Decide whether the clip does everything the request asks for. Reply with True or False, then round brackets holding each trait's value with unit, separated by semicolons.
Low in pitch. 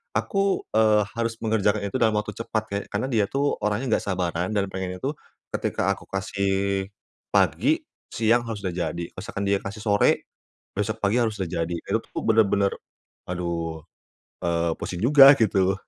True (100 Hz)